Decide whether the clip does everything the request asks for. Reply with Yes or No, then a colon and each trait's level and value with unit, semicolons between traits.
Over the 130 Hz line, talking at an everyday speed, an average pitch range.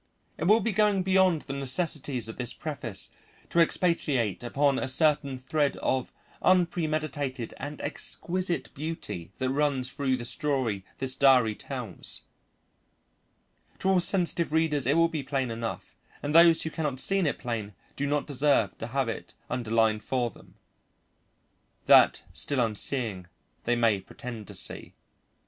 Yes: medium, 140 Hz; average, 145 wpm; average, 4.7 semitones